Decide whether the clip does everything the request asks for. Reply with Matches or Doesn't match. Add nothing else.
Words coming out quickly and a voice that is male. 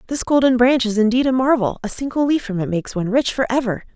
Doesn't match